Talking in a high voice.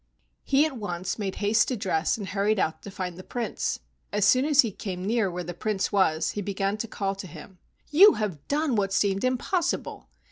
Yes: high, 205 Hz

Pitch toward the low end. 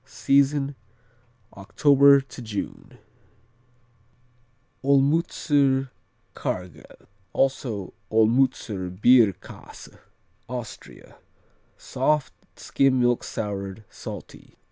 Yes: low, 130 Hz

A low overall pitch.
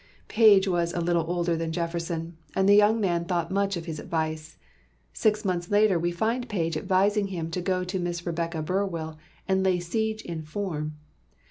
No: medium, 175 Hz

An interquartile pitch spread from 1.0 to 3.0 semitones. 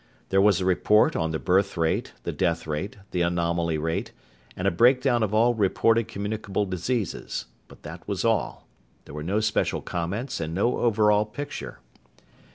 No: average, 4.2 semitones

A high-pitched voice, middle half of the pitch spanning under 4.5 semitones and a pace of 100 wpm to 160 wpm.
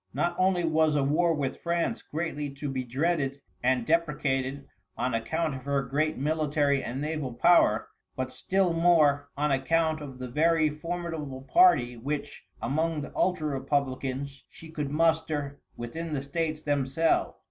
No: medium, 150 Hz; average, 3.2 semitones; average, 150 wpm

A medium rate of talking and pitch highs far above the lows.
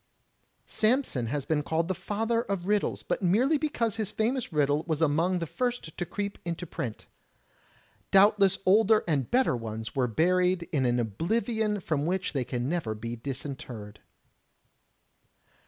Yes: average, 150 wpm; wide, 7.4 semitones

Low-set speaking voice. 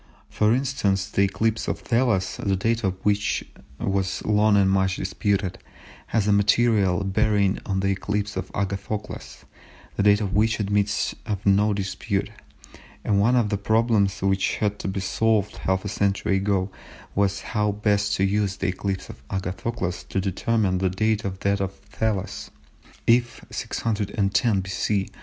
Yes: low, 100 Hz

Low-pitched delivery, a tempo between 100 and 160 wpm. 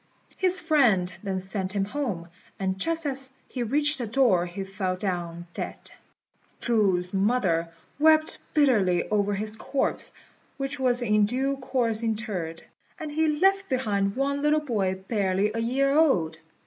No: high, 225 Hz; average, 150 wpm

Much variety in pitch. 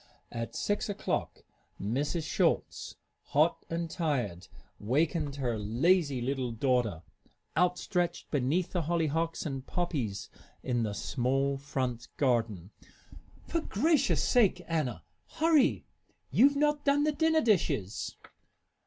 Yes: wide, 6.8 semitones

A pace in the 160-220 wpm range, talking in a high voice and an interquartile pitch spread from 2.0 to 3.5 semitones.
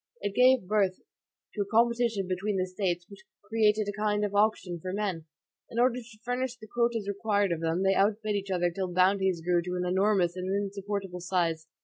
Yes: average, 200 wpm; high, 200 Hz; average, 2.8 semitones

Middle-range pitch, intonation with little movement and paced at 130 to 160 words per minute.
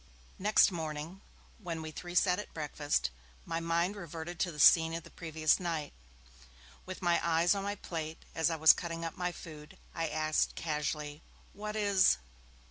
No: medium, 165 Hz; narrow, 2.2 semitones; average, 170 wpm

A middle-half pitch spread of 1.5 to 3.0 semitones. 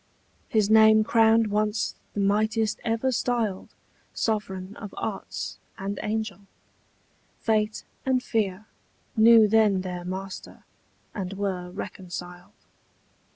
Yes: narrow, 2.4 semitones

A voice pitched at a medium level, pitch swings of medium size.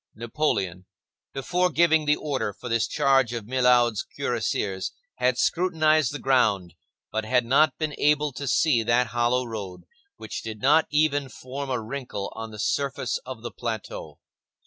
No: low, 125 Hz; average, 4.7 semitones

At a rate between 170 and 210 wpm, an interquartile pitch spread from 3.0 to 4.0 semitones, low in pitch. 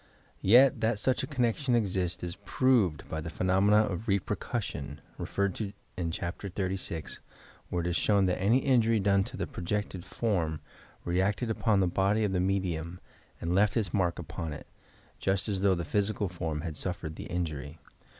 Yes: average, 175 wpm; average, 3.5 semitones; very low, 95 Hz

